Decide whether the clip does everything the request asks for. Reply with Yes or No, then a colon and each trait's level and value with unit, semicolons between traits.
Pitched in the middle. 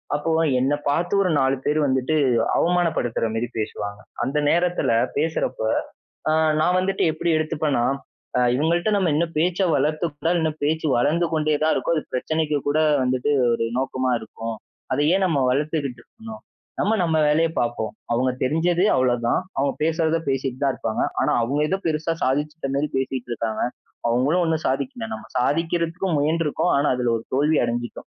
Yes: medium, 150 Hz